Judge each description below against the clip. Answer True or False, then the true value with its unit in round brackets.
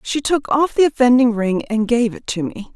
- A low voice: False (240 Hz)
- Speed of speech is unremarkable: False (240 wpm)